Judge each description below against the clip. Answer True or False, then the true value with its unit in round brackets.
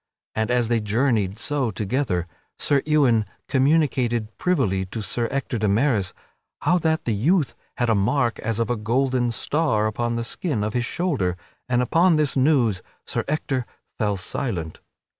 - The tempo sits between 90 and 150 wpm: False (165 wpm)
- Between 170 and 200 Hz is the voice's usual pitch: False (120 Hz)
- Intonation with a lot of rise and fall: False (4.6 semitones)